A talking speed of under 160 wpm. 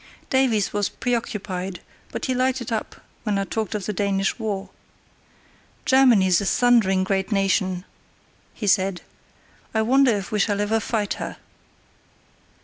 Yes: average, 140 wpm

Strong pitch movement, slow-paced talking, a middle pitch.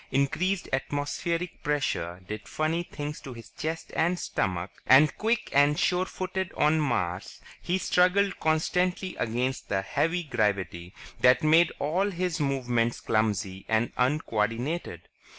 Yes: wide, 7.0 semitones; slow, 130 wpm; medium, 145 Hz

